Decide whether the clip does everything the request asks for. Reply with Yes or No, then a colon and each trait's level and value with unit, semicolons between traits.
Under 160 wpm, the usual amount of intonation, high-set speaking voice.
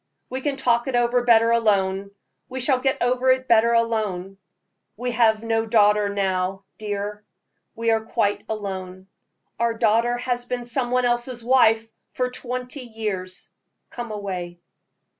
Yes: average, 145 wpm; average, 3.0 semitones; high, 230 Hz